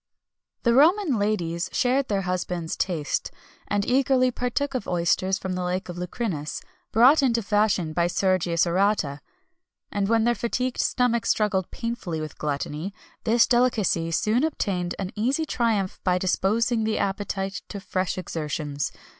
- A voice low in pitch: No, high, 200 Hz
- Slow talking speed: No, average, 145 wpm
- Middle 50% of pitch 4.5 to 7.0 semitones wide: Yes, average, 4.9 semitones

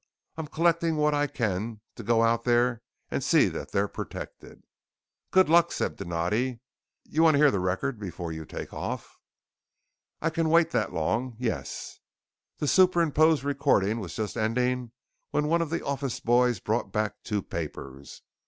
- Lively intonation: Yes, wide, 6.2 semitones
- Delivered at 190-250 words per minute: No, average, 155 wpm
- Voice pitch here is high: No, low, 125 Hz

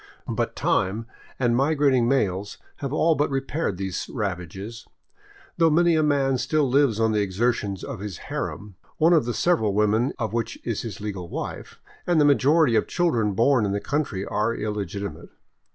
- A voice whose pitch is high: No, low, 115 Hz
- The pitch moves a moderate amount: No, wide, 5.8 semitones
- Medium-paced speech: Yes, average, 170 wpm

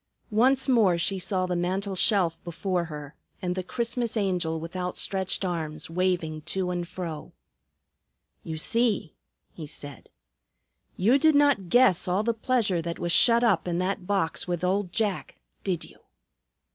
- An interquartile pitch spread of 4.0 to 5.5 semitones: No, average, 3.5 semitones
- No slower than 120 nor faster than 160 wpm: Yes, average, 155 wpm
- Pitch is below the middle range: No, medium, 185 Hz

